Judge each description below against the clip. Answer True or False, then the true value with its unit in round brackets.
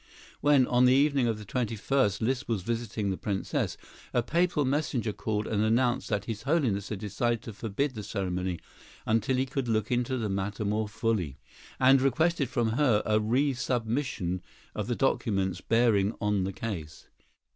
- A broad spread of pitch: False (3.8 semitones)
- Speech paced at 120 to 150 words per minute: False (165 wpm)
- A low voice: True (115 Hz)